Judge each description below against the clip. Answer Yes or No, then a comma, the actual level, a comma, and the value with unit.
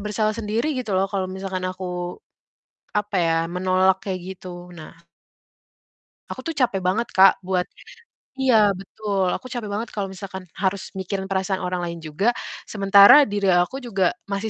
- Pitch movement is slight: Yes, narrow, 2.2 semitones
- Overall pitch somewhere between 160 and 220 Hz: Yes, high, 190 Hz